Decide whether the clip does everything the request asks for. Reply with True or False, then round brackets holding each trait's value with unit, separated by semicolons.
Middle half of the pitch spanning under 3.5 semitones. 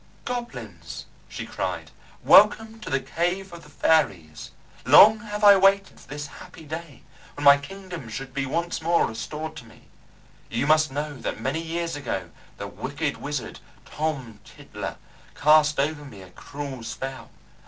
False (4.0 semitones)